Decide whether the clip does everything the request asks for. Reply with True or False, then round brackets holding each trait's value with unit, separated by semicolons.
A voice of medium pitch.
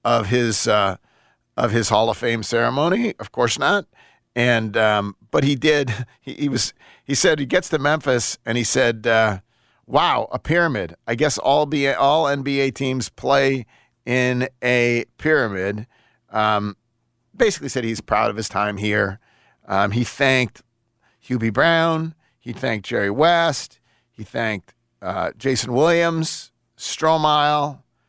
False (120 Hz)